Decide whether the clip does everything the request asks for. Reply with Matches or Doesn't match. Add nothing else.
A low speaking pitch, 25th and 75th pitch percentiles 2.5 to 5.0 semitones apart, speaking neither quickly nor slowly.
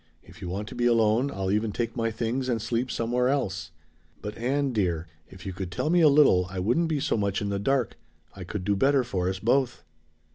Doesn't match